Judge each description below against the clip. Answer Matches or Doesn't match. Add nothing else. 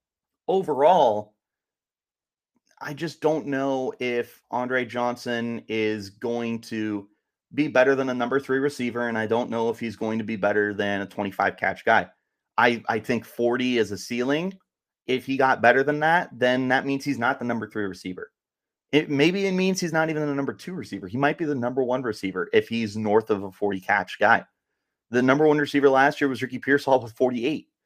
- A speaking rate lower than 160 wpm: Doesn't match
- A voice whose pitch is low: Matches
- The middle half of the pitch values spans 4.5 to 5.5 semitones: Doesn't match